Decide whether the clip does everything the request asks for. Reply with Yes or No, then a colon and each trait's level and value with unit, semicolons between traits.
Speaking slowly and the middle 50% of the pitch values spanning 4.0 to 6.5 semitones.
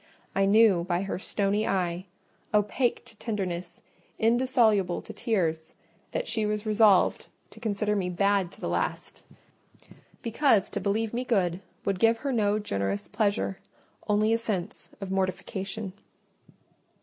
No: slow, 130 wpm; average, 2.9 semitones